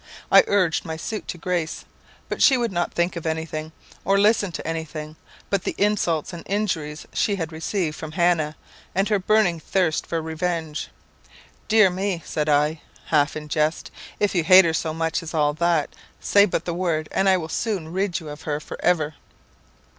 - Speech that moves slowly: No, average, 190 wpm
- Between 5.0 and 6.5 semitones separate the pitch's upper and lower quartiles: No, average, 3.3 semitones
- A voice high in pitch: No, medium, 165 Hz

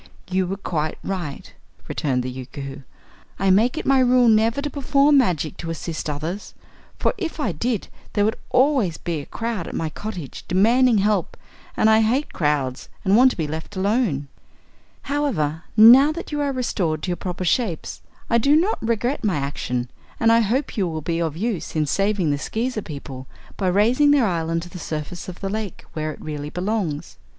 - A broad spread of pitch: Yes, wide, 7.1 semitones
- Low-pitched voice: No, high, 195 Hz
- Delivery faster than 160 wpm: Yes, average, 190 wpm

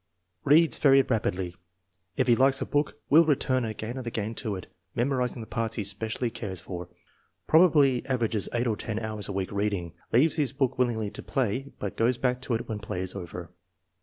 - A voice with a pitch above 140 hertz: No, low, 115 Hz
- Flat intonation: No, average, 4.4 semitones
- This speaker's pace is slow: No, average, 200 wpm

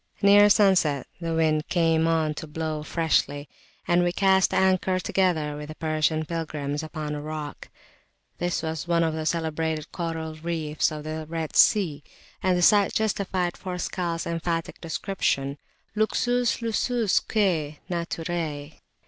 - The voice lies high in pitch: No, medium, 165 Hz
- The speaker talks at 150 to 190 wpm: No, slow, 135 wpm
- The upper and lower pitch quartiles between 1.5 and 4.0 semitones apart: Yes, average, 2.8 semitones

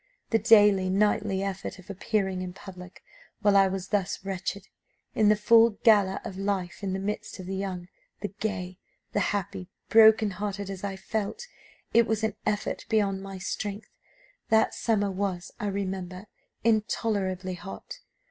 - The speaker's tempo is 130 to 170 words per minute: Yes, average, 155 wpm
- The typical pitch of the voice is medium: No, high, 200 Hz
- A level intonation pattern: Yes, narrow, 1.9 semitones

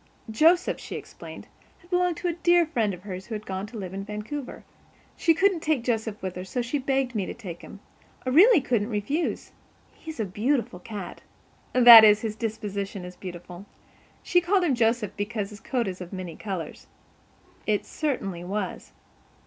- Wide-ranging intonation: Yes, wide, 6.2 semitones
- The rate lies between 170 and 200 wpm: Yes, average, 180 wpm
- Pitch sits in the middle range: No, high, 220 Hz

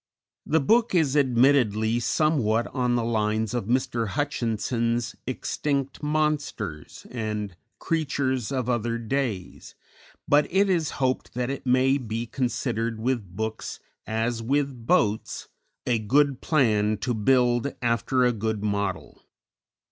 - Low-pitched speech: Yes, low, 120 Hz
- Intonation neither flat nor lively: Yes, average, 3.8 semitones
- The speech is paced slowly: Yes, slow, 125 wpm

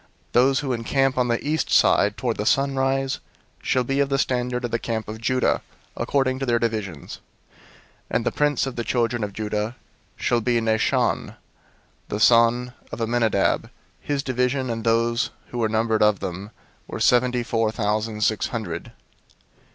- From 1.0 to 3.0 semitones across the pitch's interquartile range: Yes, average, 2.7 semitones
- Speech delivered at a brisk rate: No, average, 170 wpm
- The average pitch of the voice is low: Yes, low, 120 Hz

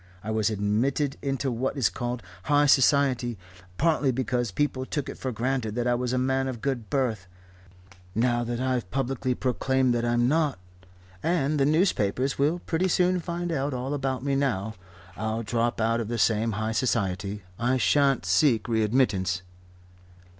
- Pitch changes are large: No, average, 3.4 semitones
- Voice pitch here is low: Yes, low, 125 Hz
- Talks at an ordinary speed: Yes, average, 165 wpm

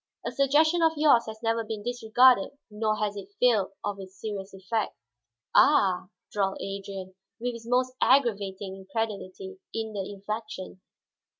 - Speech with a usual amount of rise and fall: Yes, average, 3.8 semitones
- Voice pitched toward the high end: Yes, high, 215 Hz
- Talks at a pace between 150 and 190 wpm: No, average, 140 wpm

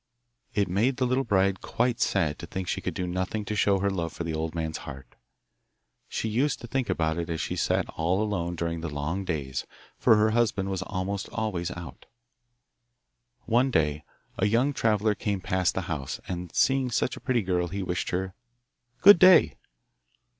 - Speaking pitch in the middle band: No, very low, 95 Hz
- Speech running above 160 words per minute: Yes, average, 190 wpm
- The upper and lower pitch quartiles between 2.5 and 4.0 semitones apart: No, average, 4.6 semitones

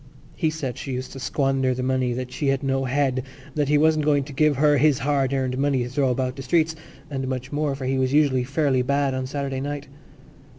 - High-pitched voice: No, low, 135 Hz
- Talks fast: Yes, fast, 240 wpm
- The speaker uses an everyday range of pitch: No, narrow, 1.9 semitones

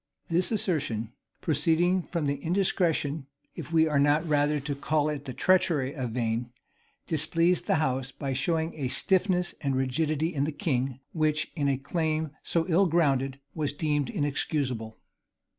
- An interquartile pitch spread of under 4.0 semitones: Yes, average, 3.3 semitones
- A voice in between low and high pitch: Yes, medium, 150 Hz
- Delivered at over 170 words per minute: No, average, 155 wpm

